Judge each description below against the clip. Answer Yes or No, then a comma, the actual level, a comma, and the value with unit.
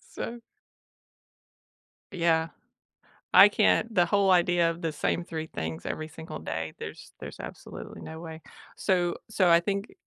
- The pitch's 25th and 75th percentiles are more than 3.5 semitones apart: No, narrow, 2.6 semitones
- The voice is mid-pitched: Yes, medium, 170 Hz